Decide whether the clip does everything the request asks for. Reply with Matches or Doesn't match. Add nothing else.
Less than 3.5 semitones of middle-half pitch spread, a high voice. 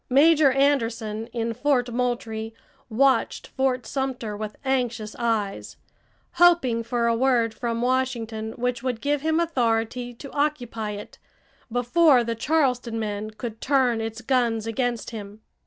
Matches